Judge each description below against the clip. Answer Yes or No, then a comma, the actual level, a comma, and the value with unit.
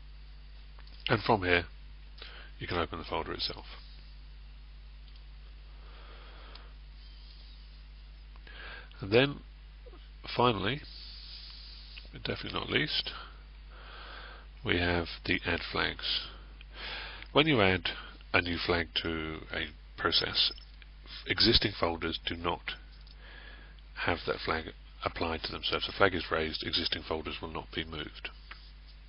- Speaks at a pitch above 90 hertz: No, very low, 75 Hz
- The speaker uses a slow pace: Yes, slow, 105 wpm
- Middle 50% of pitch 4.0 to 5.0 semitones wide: No, narrow, 2.4 semitones